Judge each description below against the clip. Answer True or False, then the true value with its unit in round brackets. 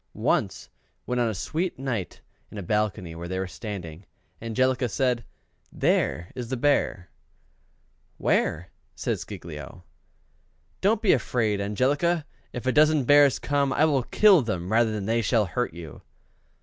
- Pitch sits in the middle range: False (115 Hz)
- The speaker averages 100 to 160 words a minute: True (150 wpm)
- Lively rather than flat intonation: True (6.1 semitones)